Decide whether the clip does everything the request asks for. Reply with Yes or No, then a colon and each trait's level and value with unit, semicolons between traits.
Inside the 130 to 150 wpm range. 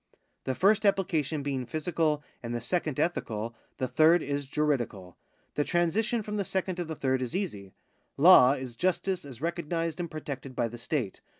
No: average, 175 wpm